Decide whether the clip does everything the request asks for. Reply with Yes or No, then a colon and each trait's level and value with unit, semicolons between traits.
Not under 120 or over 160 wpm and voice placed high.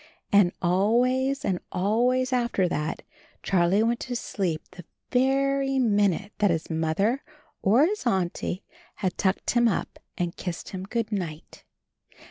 Yes: slow, 135 wpm; high, 205 Hz